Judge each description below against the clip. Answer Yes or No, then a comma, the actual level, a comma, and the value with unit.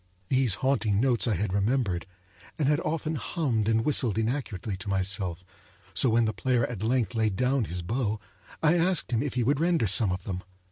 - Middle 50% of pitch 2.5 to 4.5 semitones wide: No, average, 5.0 semitones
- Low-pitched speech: Yes, low, 115 Hz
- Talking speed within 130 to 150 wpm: No, average, 195 wpm